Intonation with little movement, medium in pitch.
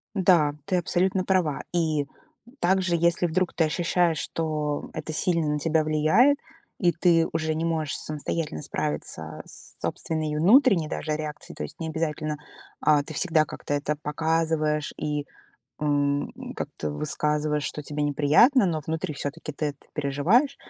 Yes: narrow, 2.3 semitones; medium, 155 Hz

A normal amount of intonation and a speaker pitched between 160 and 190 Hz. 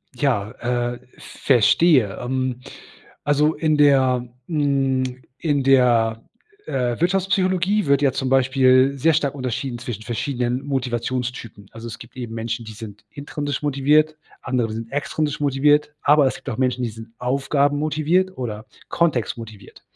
No: average, 3.4 semitones; low, 130 Hz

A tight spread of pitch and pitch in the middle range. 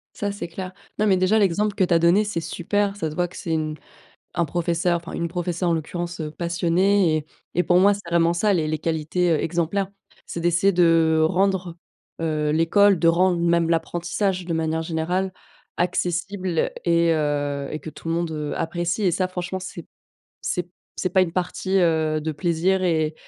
Yes: narrow, 2.3 semitones; medium, 170 Hz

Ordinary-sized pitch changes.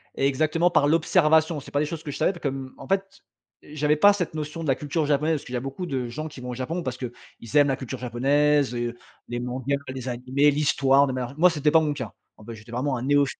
Yes: average, 3.1 semitones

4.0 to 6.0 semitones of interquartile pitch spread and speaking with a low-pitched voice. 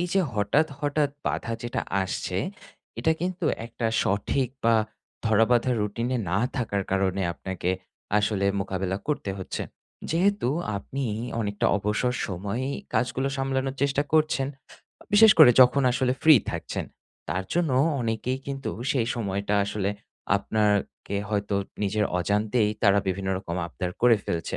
Yes: average, 5.1 semitones; low, 115 Hz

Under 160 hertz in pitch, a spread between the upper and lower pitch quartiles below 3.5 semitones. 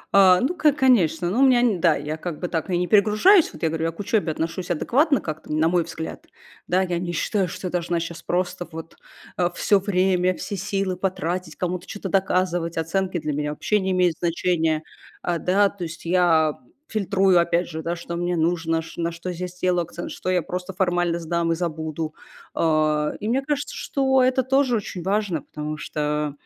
No: medium, 175 Hz; average, 2.8 semitones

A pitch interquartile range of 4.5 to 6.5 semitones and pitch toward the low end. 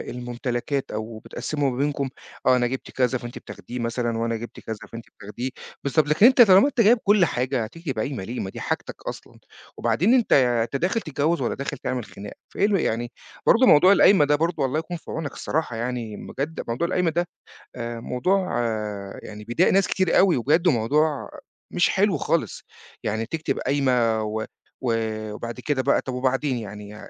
Yes: wide, 5.6 semitones; low, 130 Hz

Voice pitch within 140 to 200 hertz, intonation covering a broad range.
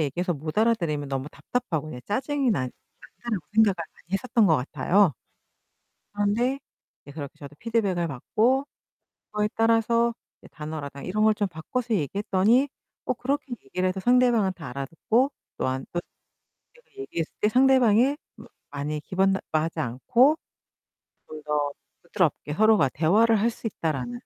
Yes: high, 195 Hz; wide, 7.2 semitones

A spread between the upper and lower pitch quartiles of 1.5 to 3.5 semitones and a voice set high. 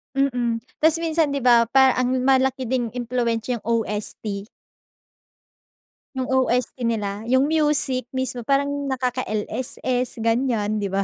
Yes: narrow, 2.5 semitones; very high, 250 Hz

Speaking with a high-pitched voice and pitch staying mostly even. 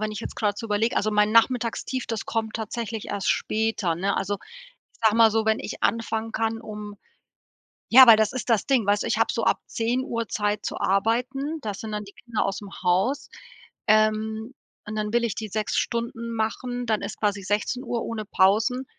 Yes: high, 220 Hz; narrow, 1.9 semitones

